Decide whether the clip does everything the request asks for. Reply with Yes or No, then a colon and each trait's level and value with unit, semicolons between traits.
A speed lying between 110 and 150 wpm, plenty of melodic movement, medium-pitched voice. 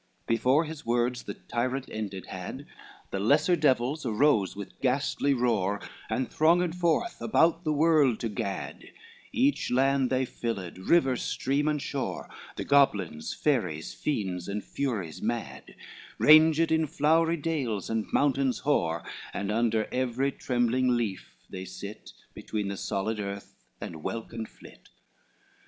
No: average, 140 wpm; wide, 5.9 semitones; low, 125 Hz